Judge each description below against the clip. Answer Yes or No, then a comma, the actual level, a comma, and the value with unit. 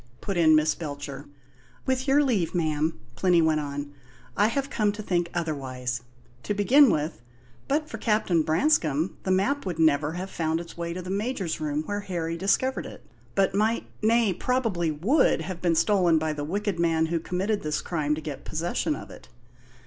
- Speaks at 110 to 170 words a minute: No, average, 185 wpm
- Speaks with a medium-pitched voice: Yes, medium, 175 Hz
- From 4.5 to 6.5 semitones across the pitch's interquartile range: Yes, average, 4.8 semitones